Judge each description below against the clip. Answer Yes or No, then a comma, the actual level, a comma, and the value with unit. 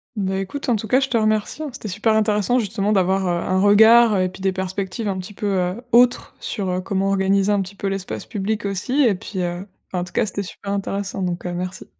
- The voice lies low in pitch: No, high, 200 Hz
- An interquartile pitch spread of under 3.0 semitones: Yes, narrow, 2.4 semitones